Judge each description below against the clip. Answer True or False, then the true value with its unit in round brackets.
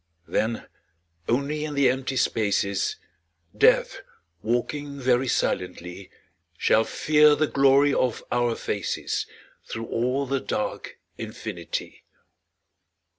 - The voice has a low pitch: True (130 Hz)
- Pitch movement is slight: False (3.8 semitones)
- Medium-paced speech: False (100 wpm)